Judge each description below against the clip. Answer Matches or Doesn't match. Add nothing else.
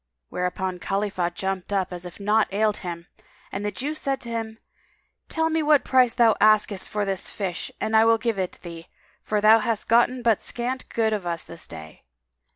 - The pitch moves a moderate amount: Matches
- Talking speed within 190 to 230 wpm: Matches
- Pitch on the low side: Doesn't match